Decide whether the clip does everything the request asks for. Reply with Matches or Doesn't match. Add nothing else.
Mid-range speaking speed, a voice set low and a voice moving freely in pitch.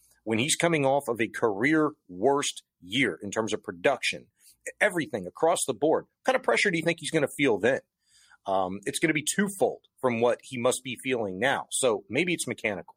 Doesn't match